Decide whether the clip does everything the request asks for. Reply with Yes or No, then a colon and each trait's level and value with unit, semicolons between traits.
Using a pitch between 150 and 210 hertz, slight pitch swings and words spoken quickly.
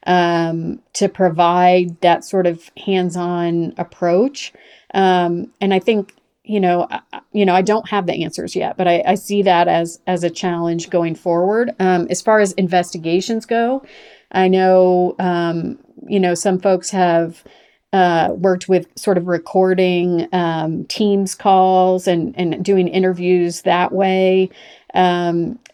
No: medium, 185 Hz; narrow, 1.9 semitones; average, 150 wpm